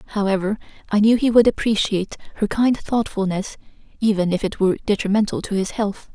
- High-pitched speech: Yes, high, 210 Hz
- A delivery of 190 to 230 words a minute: No, average, 165 wpm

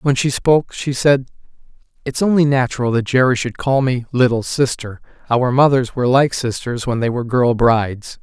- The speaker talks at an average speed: Yes, average, 180 wpm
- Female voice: No, male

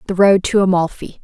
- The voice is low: No, high, 190 Hz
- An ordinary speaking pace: Yes, average, 195 wpm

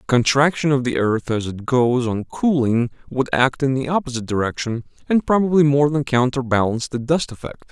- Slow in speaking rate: No, average, 180 wpm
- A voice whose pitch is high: No, low, 130 Hz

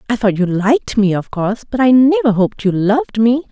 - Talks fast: Yes, fast, 240 wpm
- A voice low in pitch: No, high, 225 Hz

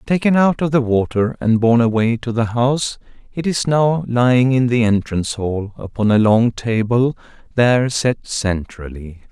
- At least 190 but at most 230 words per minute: No, average, 170 wpm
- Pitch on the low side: Yes, low, 120 Hz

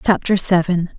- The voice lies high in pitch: No, medium, 180 Hz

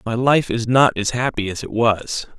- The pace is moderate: No, fast, 225 wpm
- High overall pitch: No, low, 120 Hz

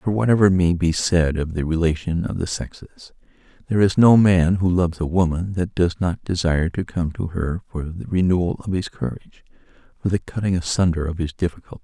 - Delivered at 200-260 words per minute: Yes, fast, 205 wpm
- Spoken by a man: Yes, male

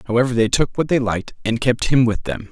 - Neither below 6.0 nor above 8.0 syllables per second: Yes, 6.3 syllables/s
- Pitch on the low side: Yes, low, 120 Hz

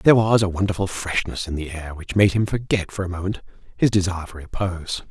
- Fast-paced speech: Yes, fast, 225 wpm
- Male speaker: Yes, male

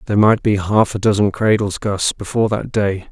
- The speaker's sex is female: No, male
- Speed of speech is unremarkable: No, fast, 210 wpm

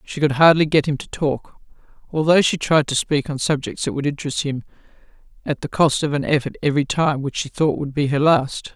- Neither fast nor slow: No, fast, 225 wpm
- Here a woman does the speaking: Yes, female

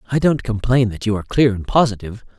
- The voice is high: No, low, 115 Hz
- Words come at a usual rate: No, fast, 225 wpm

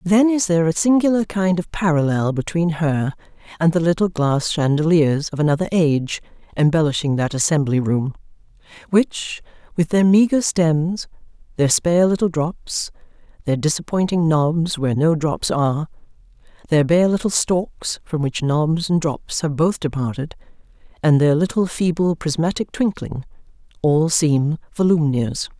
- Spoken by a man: No, female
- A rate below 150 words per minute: Yes, average, 140 wpm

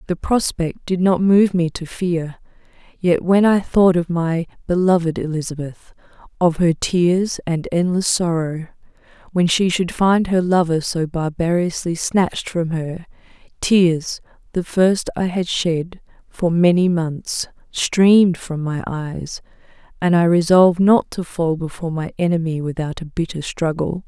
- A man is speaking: No, female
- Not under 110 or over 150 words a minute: Yes, average, 145 wpm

